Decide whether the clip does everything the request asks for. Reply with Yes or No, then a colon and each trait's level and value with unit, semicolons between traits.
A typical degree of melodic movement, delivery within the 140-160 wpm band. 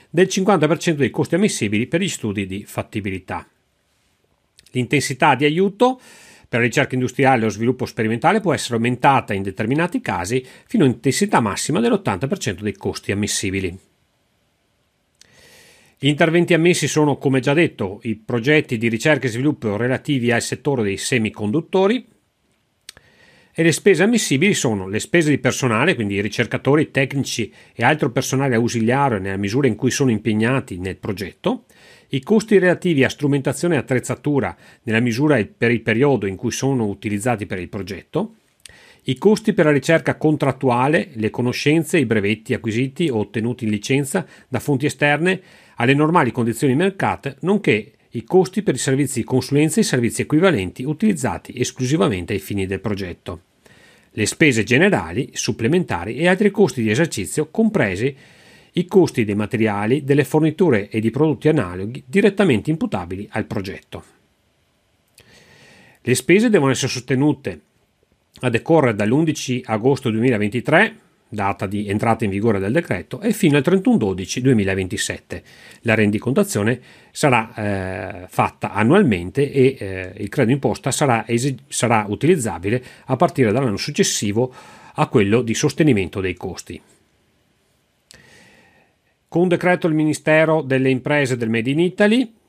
No: wide, 6.0 semitones; average, 145 wpm